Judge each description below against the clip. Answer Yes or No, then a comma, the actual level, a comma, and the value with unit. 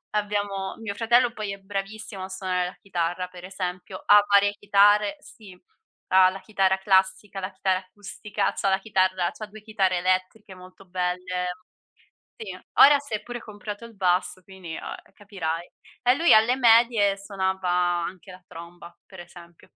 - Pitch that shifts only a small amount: Yes, narrow, 2.2 semitones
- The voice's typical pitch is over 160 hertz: Yes, high, 190 Hz